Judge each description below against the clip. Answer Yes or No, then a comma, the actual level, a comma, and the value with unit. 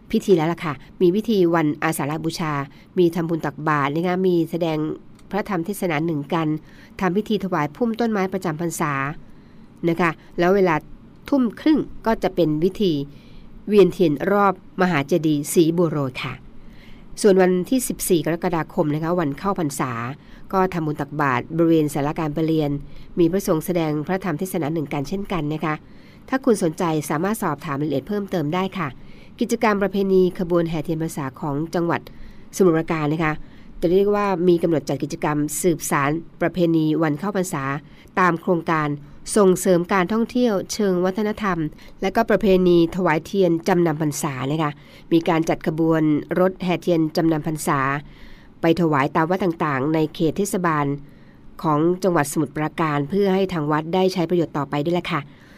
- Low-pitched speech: No, medium, 170 Hz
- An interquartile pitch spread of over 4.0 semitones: No, average, 3.4 semitones